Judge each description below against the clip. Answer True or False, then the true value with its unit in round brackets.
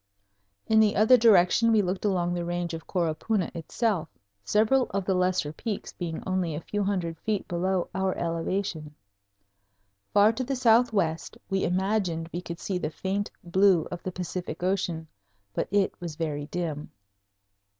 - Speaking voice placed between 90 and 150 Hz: False (185 Hz)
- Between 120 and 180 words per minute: True (160 wpm)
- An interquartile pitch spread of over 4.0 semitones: False (3.3 semitones)